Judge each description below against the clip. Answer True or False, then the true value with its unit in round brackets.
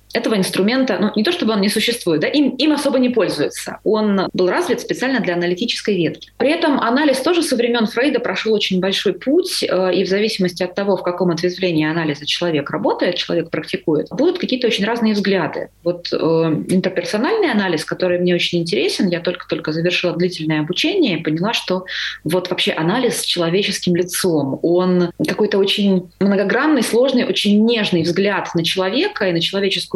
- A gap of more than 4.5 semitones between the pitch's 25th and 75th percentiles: True (4.9 semitones)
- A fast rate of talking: True (175 wpm)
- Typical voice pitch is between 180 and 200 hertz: True (190 Hz)